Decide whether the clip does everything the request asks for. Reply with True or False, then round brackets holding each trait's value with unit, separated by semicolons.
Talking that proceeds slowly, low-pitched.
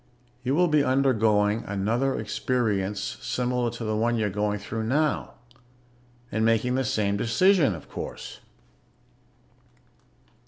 True (120 wpm; 115 Hz)